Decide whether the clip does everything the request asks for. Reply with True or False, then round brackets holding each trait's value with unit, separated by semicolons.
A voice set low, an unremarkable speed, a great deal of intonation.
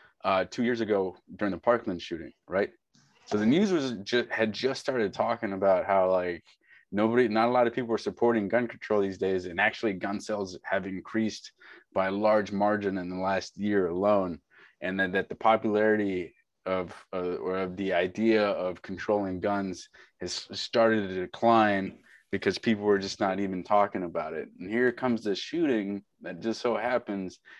False (105 Hz; 185 wpm; 2.9 semitones)